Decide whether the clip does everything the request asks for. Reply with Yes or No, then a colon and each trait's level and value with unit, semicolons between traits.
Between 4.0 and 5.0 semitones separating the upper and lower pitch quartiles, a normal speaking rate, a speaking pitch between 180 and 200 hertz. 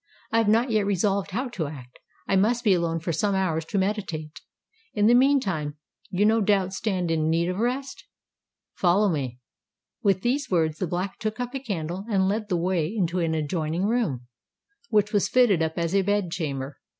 Yes: average, 4.5 semitones; average, 195 wpm; high, 190 Hz